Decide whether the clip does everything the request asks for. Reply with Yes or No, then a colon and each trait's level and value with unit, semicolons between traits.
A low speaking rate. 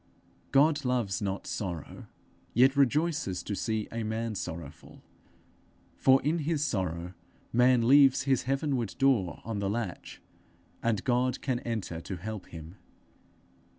Yes: slow, 130 wpm